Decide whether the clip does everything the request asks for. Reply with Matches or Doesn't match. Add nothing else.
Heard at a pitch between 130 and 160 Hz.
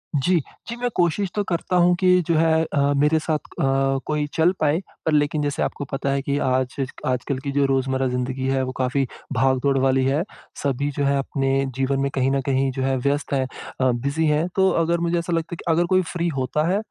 Matches